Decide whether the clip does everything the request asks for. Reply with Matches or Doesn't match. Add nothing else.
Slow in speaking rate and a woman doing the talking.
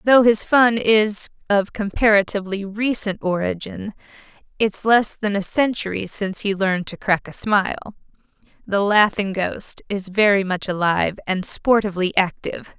Matches